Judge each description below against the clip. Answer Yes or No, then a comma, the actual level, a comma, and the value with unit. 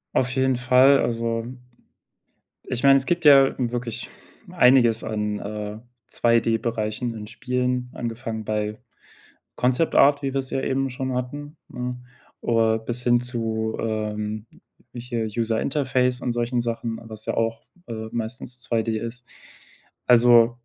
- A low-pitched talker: Yes, low, 120 Hz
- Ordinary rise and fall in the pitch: No, narrow, 2.1 semitones